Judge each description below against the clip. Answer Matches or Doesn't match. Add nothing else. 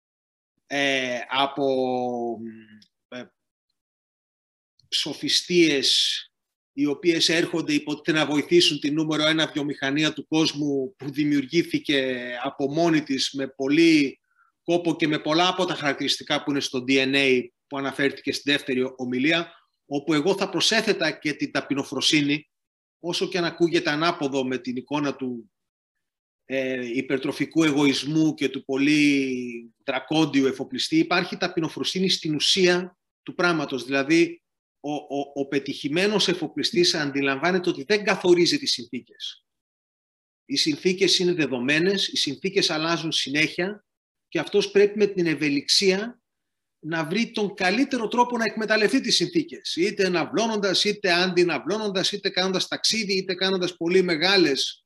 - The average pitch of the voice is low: Doesn't match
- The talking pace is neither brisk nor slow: Matches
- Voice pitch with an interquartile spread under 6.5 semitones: Matches